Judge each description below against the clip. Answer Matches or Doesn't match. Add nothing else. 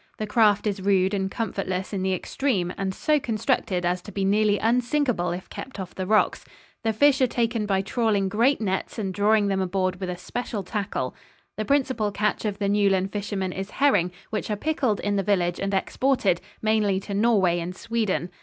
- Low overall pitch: Doesn't match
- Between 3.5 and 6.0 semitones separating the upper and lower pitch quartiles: Doesn't match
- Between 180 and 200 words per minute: Matches